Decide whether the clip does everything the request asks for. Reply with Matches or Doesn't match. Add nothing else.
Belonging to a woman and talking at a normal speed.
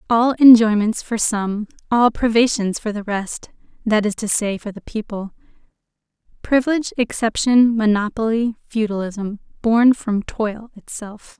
Doesn't match